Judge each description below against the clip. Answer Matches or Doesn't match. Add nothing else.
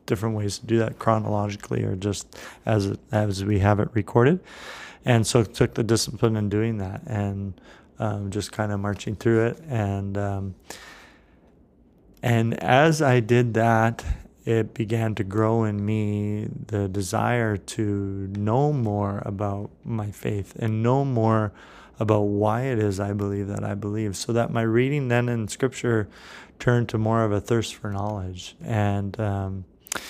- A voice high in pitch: Doesn't match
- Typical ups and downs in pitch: Doesn't match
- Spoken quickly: Doesn't match